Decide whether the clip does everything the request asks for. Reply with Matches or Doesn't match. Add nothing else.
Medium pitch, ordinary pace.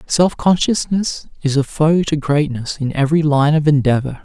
Matches